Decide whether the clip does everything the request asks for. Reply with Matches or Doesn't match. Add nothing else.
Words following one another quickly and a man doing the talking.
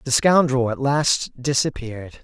Doesn't match